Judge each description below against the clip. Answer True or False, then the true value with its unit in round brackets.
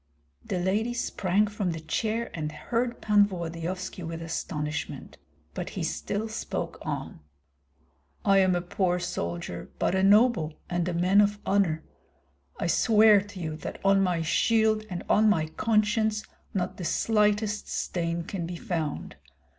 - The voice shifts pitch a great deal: False (3.9 semitones)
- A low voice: False (190 Hz)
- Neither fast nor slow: True (150 wpm)